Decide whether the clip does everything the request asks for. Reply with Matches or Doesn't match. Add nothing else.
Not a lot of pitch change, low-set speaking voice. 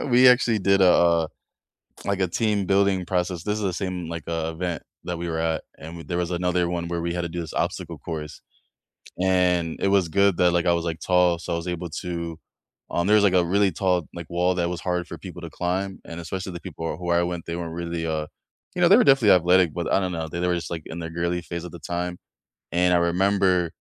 Matches